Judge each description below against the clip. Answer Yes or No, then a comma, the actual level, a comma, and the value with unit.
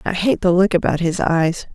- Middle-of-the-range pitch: Yes, medium, 175 Hz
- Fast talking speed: Yes, fast, 240 wpm